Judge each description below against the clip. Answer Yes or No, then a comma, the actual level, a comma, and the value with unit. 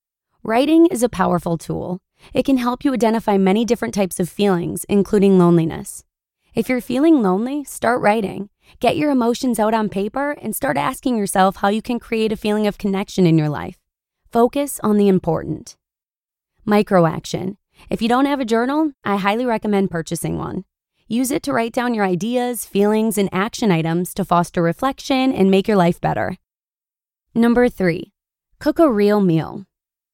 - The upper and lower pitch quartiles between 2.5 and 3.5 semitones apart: No, average, 4.5 semitones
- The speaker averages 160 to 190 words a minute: Yes, average, 170 wpm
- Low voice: No, high, 210 Hz